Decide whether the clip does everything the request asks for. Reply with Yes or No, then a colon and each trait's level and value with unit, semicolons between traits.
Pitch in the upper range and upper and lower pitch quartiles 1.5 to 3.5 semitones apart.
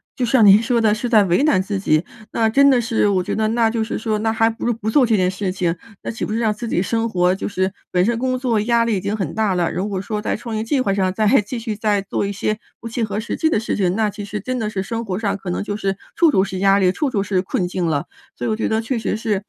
Yes: high, 215 Hz; average, 2.9 semitones